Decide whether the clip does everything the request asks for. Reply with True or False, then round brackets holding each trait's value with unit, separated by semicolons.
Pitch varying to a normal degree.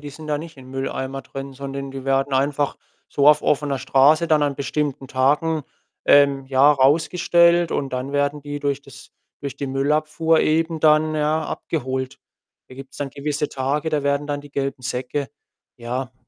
False (1.9 semitones)